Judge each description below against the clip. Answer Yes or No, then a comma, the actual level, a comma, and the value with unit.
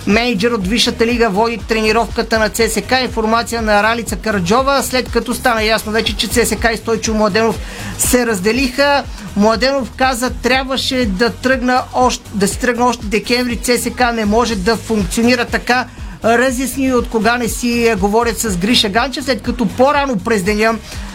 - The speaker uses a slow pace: No, average, 155 wpm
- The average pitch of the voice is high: Yes, high, 230 Hz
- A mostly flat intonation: Yes, narrow, 1.8 semitones